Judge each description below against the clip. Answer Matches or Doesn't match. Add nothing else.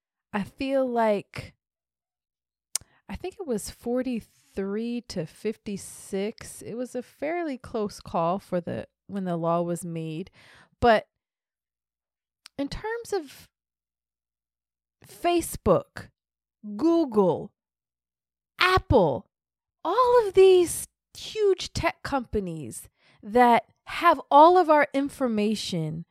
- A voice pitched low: Doesn't match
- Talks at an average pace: Doesn't match